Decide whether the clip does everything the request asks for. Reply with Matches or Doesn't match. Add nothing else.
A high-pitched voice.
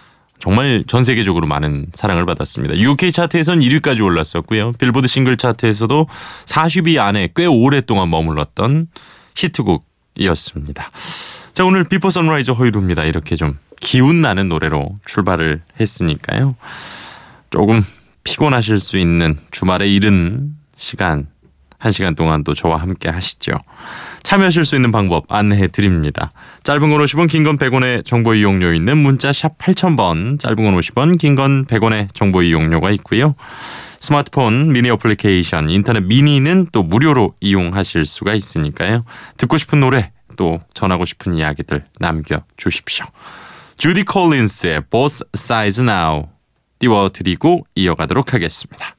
Doesn't match